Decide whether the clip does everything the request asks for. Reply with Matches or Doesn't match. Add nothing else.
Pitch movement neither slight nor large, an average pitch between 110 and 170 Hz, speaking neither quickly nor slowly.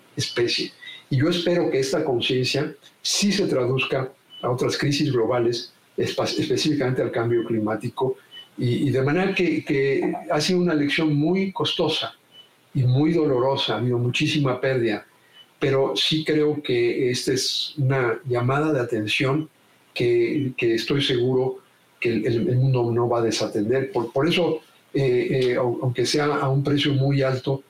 Matches